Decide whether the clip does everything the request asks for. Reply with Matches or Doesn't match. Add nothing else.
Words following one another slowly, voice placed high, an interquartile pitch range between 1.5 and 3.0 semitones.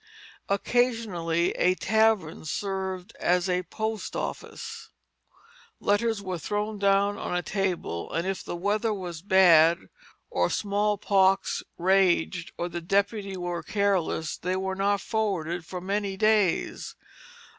Matches